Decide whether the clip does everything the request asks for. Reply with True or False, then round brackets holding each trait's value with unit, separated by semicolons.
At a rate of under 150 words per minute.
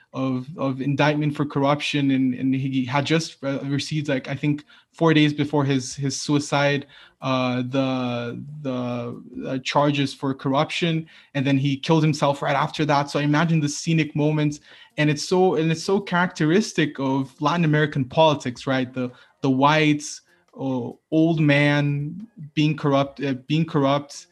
False (160 wpm)